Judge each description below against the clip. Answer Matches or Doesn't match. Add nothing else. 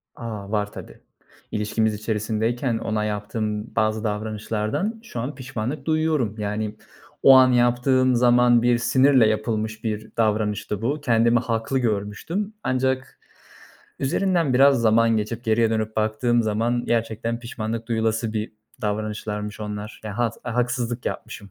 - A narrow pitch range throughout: Matches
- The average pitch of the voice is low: Matches